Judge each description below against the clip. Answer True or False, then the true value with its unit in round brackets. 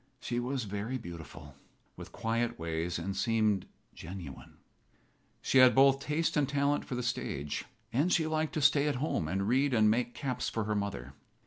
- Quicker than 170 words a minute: True (180 wpm)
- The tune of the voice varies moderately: False (6.0 semitones)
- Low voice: True (120 Hz)